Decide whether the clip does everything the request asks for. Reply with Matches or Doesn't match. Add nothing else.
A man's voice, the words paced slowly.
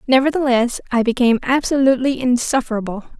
Doesn't match